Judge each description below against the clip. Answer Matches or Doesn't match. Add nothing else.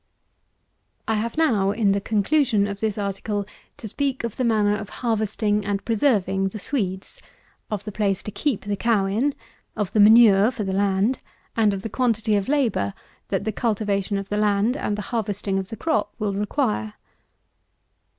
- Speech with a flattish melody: Matches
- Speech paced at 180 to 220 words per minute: Matches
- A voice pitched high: Matches